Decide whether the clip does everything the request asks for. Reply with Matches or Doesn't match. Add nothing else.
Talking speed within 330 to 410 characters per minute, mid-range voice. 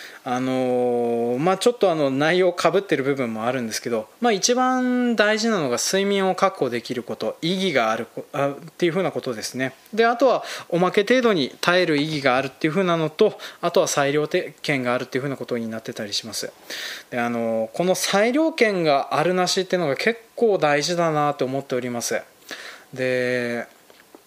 Matches